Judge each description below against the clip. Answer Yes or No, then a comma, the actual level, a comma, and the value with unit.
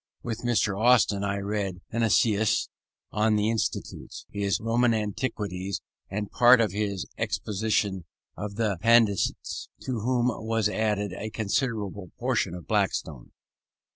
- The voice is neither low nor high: No, low, 105 Hz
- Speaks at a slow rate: Yes, slow, 125 wpm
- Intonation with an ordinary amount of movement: No, narrow, 2.3 semitones